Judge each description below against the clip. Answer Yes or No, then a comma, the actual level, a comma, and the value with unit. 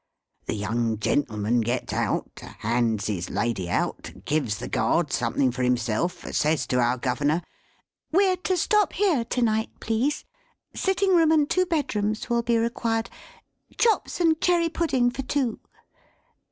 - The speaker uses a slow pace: No, average, 145 wpm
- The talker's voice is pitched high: Yes, high, 210 Hz